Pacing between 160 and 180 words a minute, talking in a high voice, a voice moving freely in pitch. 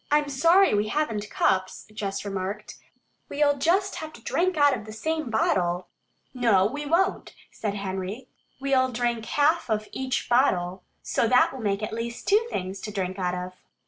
Yes: average, 175 wpm; high, 230 Hz; wide, 6.6 semitones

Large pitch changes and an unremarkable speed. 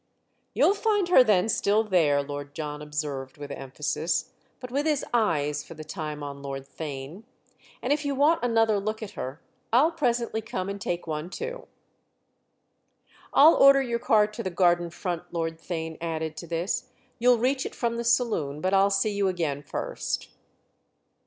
Yes: wide, 7.6 semitones; average, 170 wpm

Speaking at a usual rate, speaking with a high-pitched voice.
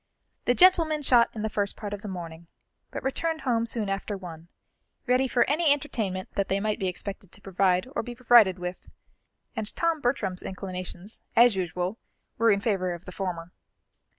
Yes: average, 180 wpm; high, 205 Hz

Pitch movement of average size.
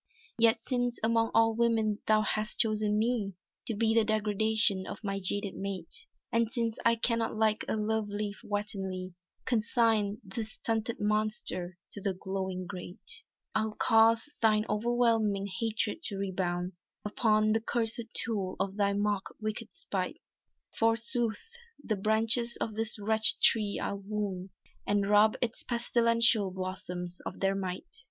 No: narrow, 2.2 semitones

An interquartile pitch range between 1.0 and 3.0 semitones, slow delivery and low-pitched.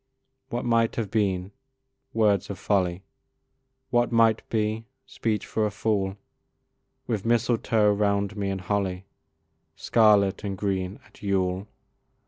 Yes: narrow, 2.4 semitones; slow, 120 wpm; low, 105 Hz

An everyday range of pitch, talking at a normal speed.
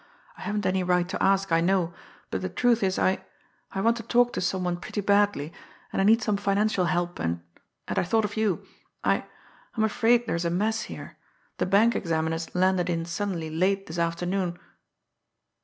Yes: average, 3.0 semitones; average, 195 wpm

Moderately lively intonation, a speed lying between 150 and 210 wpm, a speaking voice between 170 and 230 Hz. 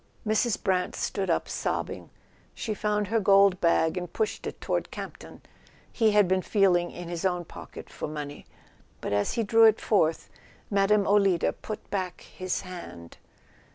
Yes: average, 3.2 semitones; average, 165 wpm; high, 190 Hz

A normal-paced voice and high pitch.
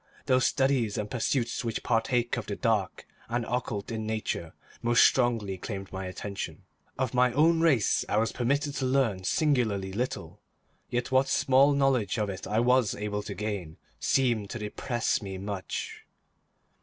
No: average, 160 wpm; low, 115 Hz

